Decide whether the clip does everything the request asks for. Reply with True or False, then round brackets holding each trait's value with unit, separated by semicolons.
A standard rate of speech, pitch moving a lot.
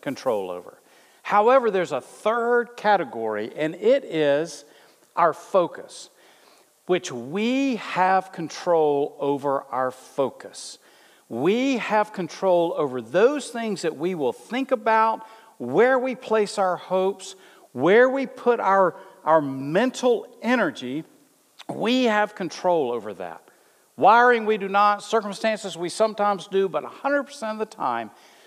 False (125 wpm; 5.9 semitones)